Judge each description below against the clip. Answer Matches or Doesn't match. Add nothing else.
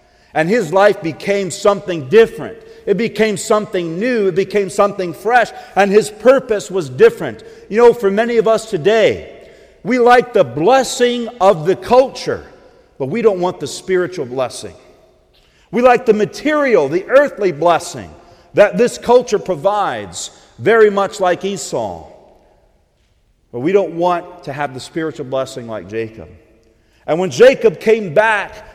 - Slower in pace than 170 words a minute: Matches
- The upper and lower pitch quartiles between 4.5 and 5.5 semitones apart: Matches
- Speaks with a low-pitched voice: Doesn't match